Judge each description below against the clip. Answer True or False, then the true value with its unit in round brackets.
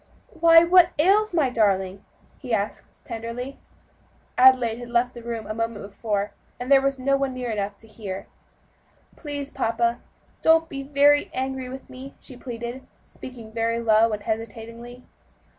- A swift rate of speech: False (155 wpm)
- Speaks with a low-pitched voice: False (240 Hz)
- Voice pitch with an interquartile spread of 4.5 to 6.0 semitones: False (3.4 semitones)